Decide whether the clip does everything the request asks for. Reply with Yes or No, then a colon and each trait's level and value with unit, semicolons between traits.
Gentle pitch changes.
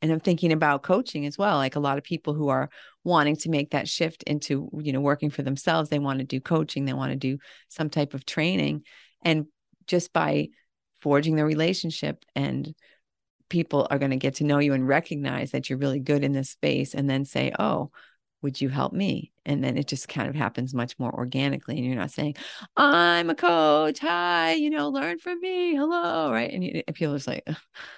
No: average, 3.3 semitones